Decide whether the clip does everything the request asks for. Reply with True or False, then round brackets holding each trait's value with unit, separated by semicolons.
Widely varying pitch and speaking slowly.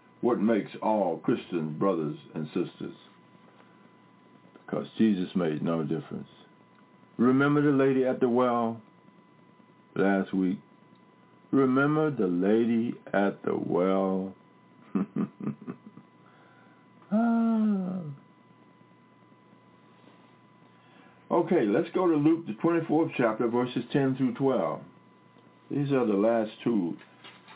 True (7.5 semitones; 95 wpm)